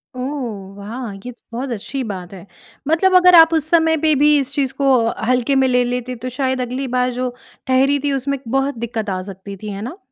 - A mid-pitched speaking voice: No, very high, 255 Hz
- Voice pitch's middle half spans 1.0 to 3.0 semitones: No, average, 3.6 semitones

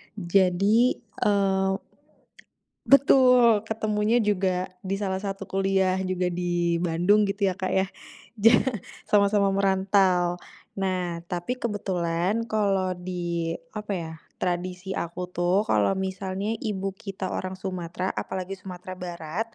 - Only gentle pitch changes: Yes, narrow, 2.2 semitones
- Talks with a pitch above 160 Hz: Yes, high, 190 Hz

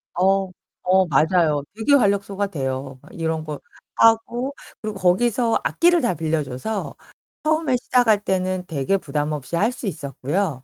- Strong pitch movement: Yes, wide, 6.6 semitones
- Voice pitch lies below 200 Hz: Yes, medium, 185 Hz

